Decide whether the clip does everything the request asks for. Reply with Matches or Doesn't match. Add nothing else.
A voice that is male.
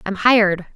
Doesn't match